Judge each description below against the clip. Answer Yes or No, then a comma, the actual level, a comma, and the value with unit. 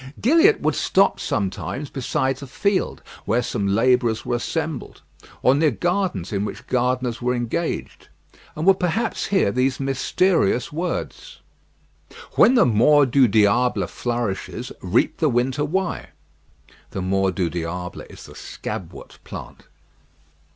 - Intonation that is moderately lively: No, wide, 7.0 semitones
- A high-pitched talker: No, low, 125 Hz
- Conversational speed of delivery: No, slow, 130 wpm